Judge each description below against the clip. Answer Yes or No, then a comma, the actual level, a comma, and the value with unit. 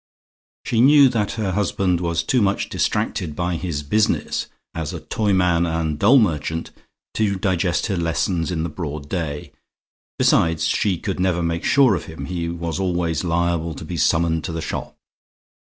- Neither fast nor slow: Yes, average, 165 wpm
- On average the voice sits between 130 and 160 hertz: No, very low, 85 Hz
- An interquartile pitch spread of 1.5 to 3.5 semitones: Yes, average, 2.8 semitones